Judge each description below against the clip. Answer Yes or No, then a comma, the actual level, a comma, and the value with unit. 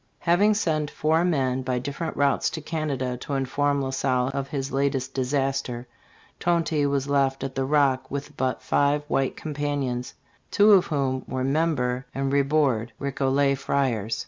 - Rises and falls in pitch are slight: Yes, narrow, 1.9 semitones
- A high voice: No, medium, 140 Hz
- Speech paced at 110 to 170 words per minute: Yes, average, 155 wpm